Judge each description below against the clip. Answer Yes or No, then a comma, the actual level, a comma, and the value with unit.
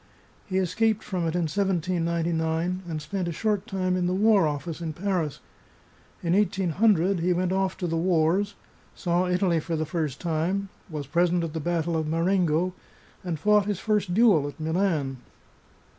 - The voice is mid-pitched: Yes, medium, 175 Hz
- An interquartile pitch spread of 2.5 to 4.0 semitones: Yes, average, 2.9 semitones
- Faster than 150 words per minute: Yes, average, 170 wpm